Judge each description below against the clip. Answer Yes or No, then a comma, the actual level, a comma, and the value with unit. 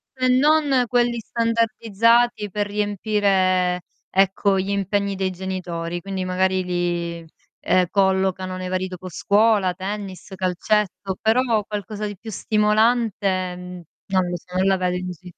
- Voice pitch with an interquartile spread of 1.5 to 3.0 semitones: Yes, narrow, 2.6 semitones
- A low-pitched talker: No, high, 195 Hz